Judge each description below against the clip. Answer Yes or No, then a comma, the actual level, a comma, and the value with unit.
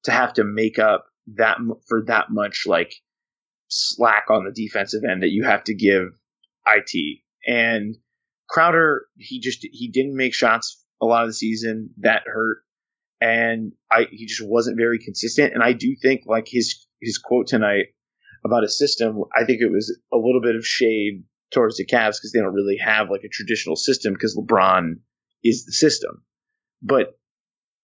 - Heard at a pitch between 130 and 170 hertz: No, low, 115 Hz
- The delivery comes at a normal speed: Yes, average, 175 wpm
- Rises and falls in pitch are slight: Yes, narrow, 1.9 semitones